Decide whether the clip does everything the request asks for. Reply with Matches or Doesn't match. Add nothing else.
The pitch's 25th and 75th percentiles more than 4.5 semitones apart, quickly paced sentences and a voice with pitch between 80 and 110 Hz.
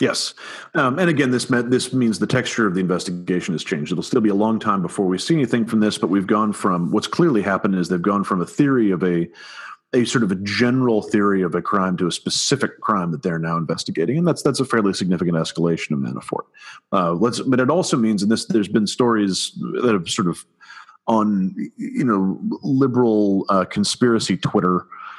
Matches